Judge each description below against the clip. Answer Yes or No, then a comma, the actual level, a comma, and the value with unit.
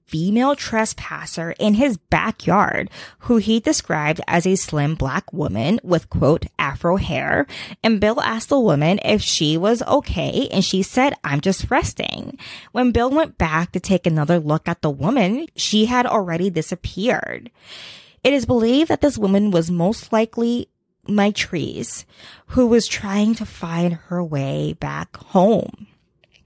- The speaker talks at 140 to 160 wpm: Yes, average, 150 wpm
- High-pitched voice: Yes, high, 200 Hz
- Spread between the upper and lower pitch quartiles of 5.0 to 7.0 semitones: Yes, wide, 5.6 semitones